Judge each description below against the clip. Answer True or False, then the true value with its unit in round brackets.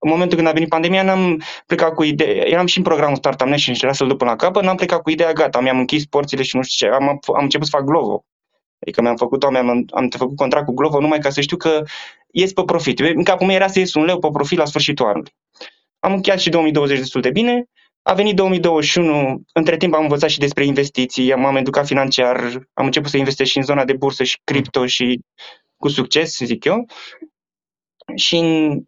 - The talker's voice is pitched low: False (150 Hz)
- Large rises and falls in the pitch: False (3.9 semitones)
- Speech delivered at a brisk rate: True (220 wpm)